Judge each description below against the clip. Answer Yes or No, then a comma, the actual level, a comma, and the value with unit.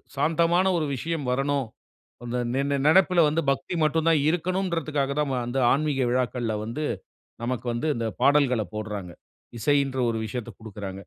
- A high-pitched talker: No, medium, 140 Hz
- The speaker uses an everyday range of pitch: Yes, average, 4.8 semitones